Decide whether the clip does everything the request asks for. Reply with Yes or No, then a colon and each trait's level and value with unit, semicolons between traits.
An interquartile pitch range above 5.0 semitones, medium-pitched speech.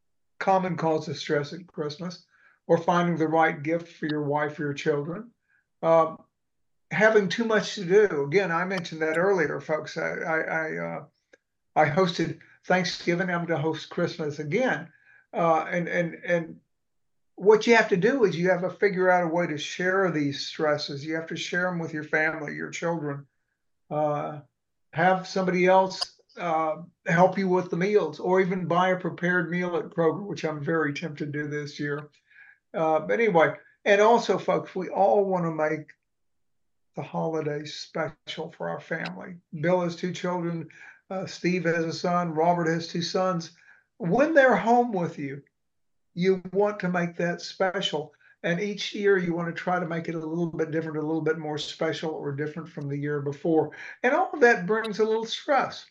No: average, 3.1 semitones; medium, 170 Hz